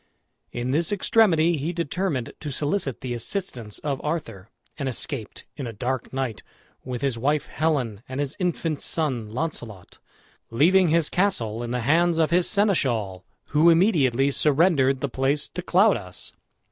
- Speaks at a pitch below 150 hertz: Yes, medium, 140 Hz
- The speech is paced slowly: No, average, 150 wpm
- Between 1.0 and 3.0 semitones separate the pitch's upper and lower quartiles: No, wide, 5.6 semitones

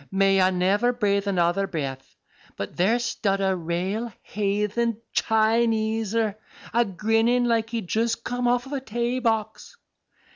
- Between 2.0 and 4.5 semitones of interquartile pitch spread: Yes, average, 3.2 semitones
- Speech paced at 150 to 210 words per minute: No, slow, 135 wpm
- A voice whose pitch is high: Yes, high, 220 Hz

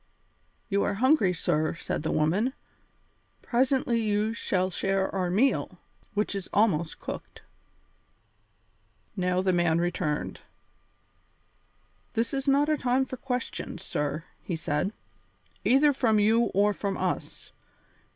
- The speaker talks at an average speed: No, slow, 120 wpm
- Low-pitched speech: No, high, 205 Hz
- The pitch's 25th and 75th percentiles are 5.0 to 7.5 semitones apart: Yes, wide, 5.5 semitones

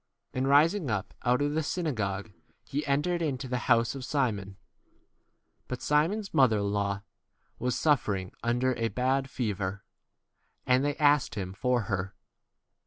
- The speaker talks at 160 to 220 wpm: No, average, 150 wpm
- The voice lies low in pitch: Yes, low, 125 Hz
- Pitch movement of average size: No, wide, 5.8 semitones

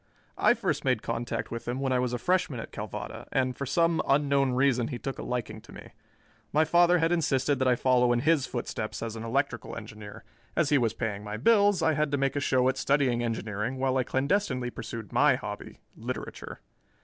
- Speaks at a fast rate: Yes, fast, 210 wpm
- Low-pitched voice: Yes, low, 130 Hz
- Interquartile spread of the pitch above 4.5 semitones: No, average, 3.6 semitones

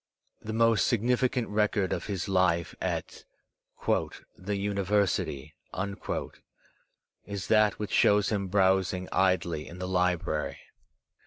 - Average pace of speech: No, slow, 105 wpm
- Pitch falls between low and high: No, low, 100 Hz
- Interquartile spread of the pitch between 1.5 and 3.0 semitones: Yes, narrow, 2.4 semitones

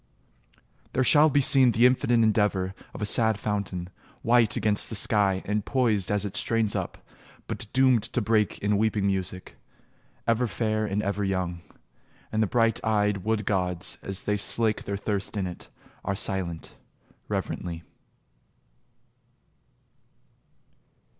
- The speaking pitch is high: No, low, 105 Hz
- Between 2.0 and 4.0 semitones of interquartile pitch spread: Yes, narrow, 2.6 semitones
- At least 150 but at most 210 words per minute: No, average, 140 wpm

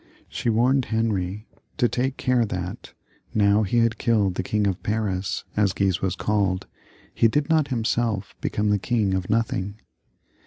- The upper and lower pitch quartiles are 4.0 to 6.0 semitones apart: No, average, 3.2 semitones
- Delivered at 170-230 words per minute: No, average, 160 wpm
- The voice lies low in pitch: Yes, low, 105 Hz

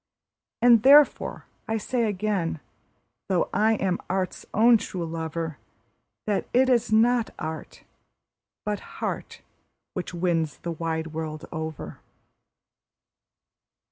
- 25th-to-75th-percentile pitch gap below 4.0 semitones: No, wide, 5.4 semitones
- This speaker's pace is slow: Yes, slow, 110 wpm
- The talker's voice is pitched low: No, medium, 185 Hz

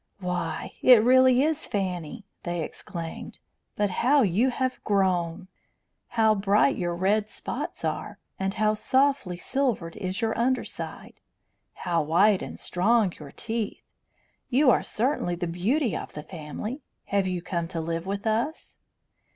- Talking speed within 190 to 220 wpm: No, average, 145 wpm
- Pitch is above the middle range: Yes, high, 200 Hz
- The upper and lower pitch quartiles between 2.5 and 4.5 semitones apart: No, average, 5.3 semitones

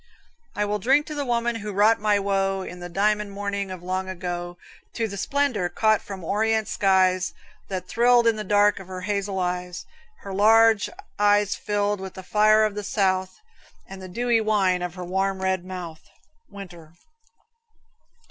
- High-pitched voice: Yes, high, 200 Hz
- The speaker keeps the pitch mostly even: Yes, narrow, 2.3 semitones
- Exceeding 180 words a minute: No, average, 175 wpm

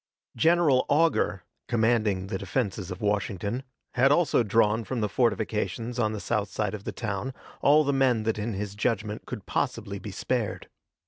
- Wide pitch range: No, average, 3.5 semitones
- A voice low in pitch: Yes, low, 110 Hz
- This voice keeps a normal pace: Yes, average, 170 wpm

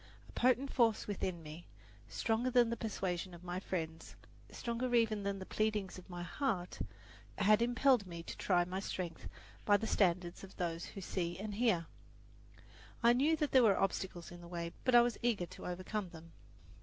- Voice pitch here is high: Yes, high, 195 Hz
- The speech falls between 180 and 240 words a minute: Yes, average, 185 wpm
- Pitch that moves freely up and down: No, average, 4.8 semitones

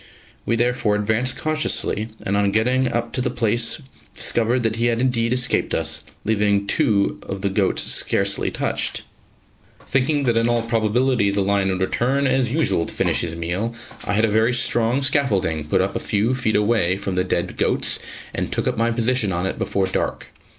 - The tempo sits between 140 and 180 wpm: No, average, 190 wpm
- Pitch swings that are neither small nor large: Yes, average, 3.6 semitones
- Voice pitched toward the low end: Yes, low, 115 Hz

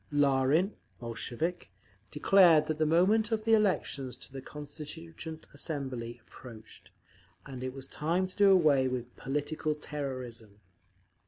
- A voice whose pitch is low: No, medium, 150 Hz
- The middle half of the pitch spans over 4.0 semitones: Yes, average, 4.4 semitones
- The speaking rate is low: Yes, slow, 130 wpm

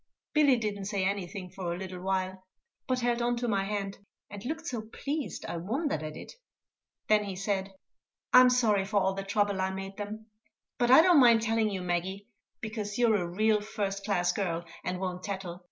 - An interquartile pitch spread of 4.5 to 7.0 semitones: No, average, 3.0 semitones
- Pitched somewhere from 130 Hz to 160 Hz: No, high, 200 Hz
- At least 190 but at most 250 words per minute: Yes, average, 195 wpm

